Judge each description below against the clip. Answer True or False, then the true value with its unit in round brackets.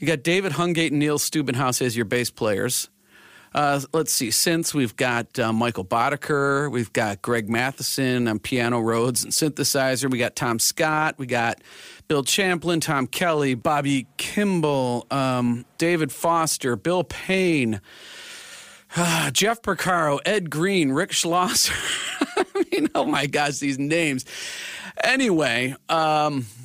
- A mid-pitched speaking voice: True (145 Hz)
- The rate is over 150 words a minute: False (135 wpm)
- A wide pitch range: False (4.9 semitones)